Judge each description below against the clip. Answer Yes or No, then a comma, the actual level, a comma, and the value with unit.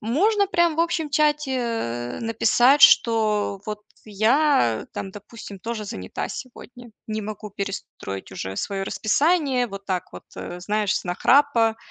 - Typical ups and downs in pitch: No, wide, 5.8 semitones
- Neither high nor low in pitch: No, high, 225 Hz